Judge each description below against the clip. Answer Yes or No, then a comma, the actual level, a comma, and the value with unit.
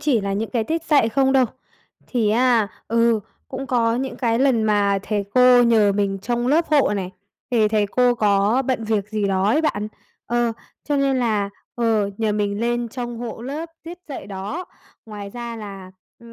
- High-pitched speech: Yes, high, 230 Hz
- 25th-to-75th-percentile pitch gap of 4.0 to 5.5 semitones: No, average, 3.3 semitones